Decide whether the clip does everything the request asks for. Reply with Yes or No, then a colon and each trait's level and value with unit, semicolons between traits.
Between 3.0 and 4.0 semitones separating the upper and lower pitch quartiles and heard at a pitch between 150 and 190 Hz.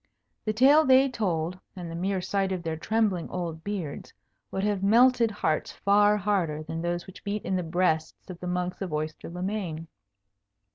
Yes: average, 3.7 semitones; medium, 185 Hz